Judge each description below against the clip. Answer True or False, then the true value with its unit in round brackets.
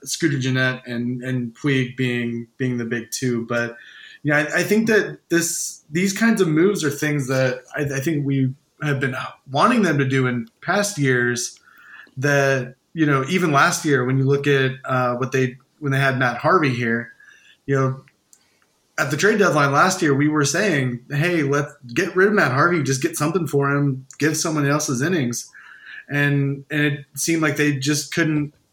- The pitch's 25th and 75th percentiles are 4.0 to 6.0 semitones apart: False (2.9 semitones)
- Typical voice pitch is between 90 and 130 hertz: False (140 Hz)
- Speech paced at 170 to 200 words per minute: True (190 wpm)